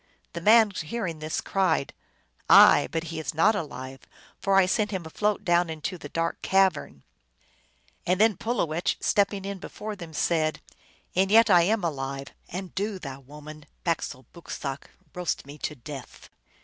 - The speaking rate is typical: Yes, average, 175 wpm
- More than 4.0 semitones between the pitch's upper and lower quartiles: Yes, average, 4.4 semitones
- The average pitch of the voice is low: No, medium, 170 Hz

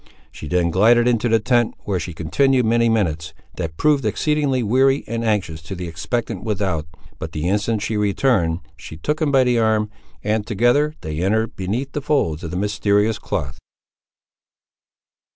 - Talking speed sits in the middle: Yes, average, 170 wpm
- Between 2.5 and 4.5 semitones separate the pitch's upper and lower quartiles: No, wide, 5.5 semitones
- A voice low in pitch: Yes, low, 105 Hz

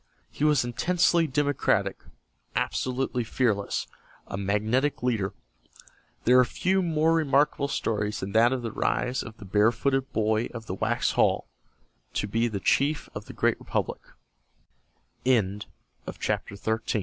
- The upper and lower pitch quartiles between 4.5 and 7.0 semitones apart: Yes, average, 4.9 semitones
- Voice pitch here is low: Yes, low, 120 Hz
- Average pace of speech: No, slow, 125 wpm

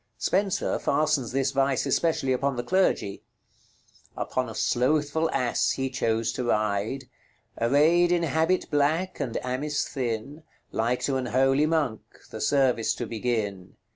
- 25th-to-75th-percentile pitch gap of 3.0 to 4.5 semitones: Yes, average, 4.2 semitones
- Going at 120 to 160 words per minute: Yes, average, 140 wpm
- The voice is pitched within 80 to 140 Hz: Yes, low, 135 Hz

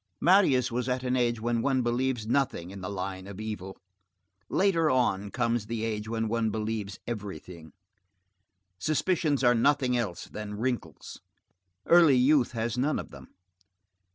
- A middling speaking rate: Yes, average, 150 wpm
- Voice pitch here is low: Yes, low, 120 Hz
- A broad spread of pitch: No, average, 3.6 semitones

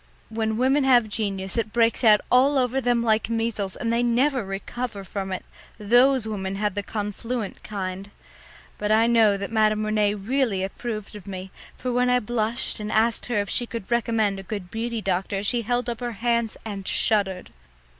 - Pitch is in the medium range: No, high, 220 Hz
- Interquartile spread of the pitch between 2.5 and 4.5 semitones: Yes, average, 2.9 semitones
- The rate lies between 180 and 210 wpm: Yes, average, 185 wpm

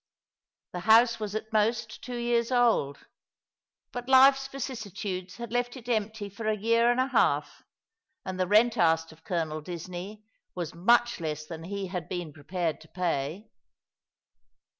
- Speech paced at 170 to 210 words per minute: No, average, 155 wpm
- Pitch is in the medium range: No, high, 205 Hz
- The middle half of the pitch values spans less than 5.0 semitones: No, average, 5.3 semitones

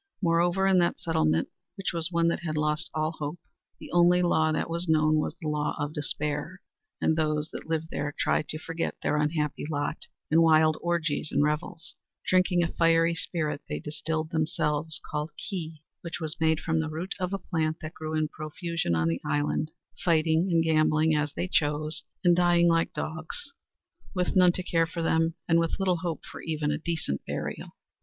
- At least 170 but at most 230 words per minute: Yes, average, 190 wpm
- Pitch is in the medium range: Yes, medium, 160 Hz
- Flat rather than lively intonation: Yes, narrow, 1.8 semitones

